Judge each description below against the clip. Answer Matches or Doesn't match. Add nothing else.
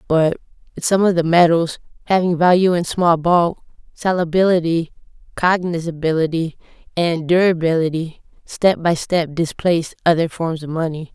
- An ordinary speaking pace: Doesn't match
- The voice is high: Doesn't match